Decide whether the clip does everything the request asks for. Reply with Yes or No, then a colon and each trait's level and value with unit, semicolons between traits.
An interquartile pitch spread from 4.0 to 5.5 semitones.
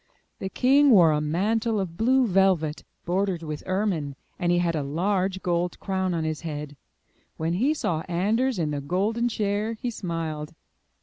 Yes: average, 4.7 semitones